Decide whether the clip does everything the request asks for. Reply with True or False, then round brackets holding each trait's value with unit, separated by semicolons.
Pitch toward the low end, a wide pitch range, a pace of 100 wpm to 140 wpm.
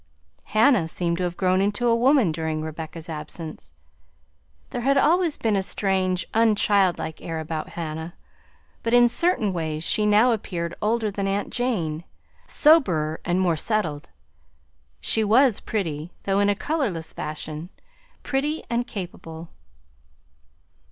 False (190 Hz; 6.0 semitones; 135 wpm)